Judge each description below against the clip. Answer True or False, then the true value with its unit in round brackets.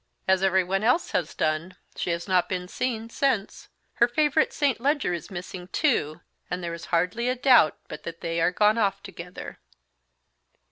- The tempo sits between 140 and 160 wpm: False (175 wpm)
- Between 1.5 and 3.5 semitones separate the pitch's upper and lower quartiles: False (5.4 semitones)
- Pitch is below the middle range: False (190 Hz)